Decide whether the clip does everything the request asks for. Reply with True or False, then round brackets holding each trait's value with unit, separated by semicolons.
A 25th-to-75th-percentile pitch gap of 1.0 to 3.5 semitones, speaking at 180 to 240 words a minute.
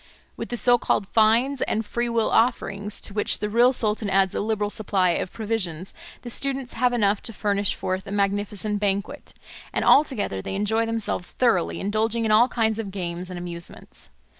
True (2.6 semitones; 185 wpm)